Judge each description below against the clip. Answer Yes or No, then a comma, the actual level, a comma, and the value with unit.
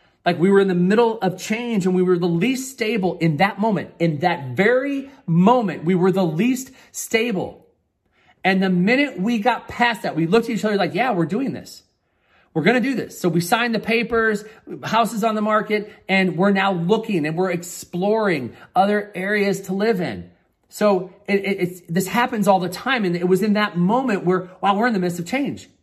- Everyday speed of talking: No, fast, 215 wpm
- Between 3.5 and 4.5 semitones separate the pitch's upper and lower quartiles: Yes, average, 4.0 semitones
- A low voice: No, high, 195 Hz